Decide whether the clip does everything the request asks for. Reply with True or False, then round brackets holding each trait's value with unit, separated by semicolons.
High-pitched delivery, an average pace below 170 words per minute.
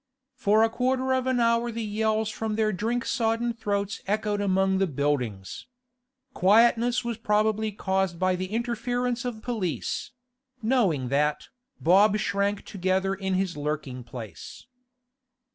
True (210 Hz; 135 wpm)